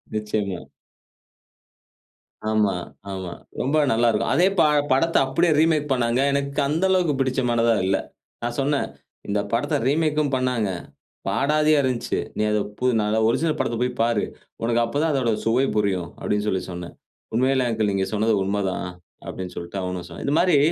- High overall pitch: No, low, 120 Hz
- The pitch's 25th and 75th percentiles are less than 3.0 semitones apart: No, average, 5.2 semitones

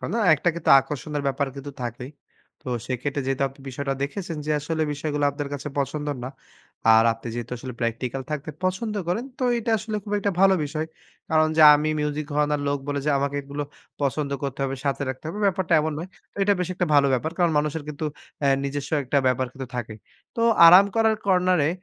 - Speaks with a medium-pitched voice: Yes, medium, 145 Hz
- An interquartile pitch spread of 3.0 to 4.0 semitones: Yes, average, 3.3 semitones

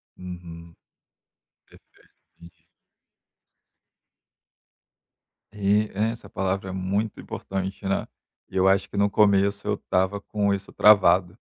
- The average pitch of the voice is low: Yes, very low, 95 Hz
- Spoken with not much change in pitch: Yes, narrow, 1.6 semitones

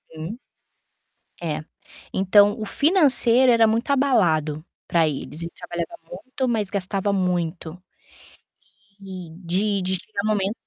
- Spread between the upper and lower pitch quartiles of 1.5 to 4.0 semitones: No, average, 4.6 semitones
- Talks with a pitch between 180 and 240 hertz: Yes, high, 195 Hz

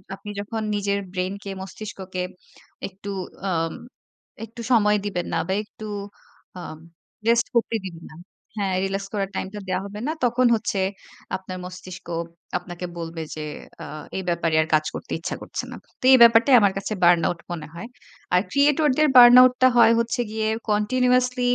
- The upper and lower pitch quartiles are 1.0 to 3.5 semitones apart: No, average, 4.2 semitones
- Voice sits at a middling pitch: No, high, 200 Hz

